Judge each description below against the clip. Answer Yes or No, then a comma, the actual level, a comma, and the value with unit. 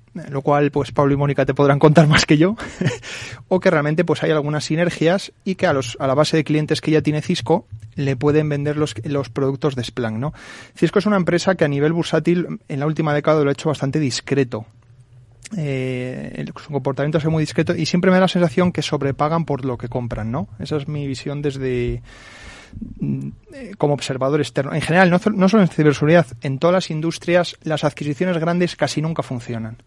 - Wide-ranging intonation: No, average, 3.5 semitones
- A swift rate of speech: Yes, fast, 205 wpm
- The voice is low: No, medium, 150 Hz